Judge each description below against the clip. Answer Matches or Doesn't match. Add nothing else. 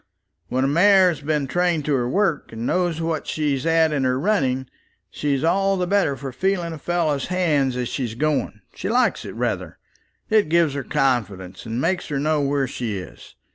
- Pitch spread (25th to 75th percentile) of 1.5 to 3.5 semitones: Doesn't match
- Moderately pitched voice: Matches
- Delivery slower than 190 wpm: Doesn't match